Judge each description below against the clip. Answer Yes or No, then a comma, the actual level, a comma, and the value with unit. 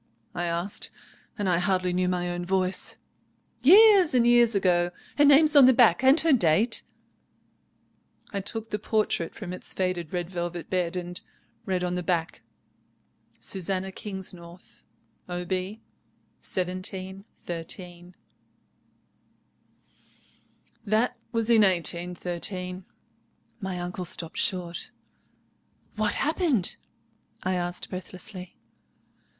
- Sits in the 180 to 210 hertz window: Yes, medium, 185 Hz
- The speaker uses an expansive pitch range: No, average, 3.3 semitones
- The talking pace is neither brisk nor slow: No, slow, 105 wpm